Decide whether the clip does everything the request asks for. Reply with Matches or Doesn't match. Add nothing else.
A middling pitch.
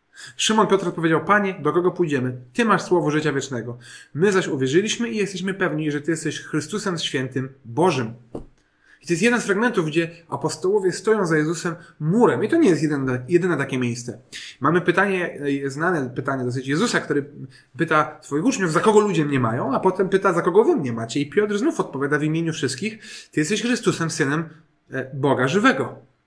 Matches